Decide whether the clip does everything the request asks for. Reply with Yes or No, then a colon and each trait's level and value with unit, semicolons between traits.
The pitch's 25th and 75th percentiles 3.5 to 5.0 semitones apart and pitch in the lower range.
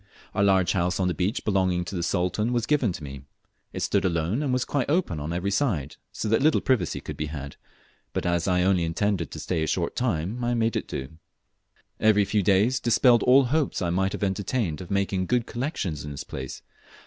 No: wide, 5.5 semitones; very low, 95 Hz